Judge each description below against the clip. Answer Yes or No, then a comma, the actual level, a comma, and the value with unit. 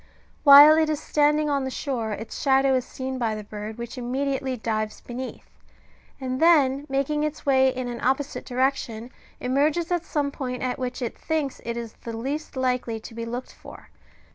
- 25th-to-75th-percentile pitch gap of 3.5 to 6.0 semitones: No, average, 2.9 semitones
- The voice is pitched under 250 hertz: No, very high, 260 Hz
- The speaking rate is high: No, average, 185 wpm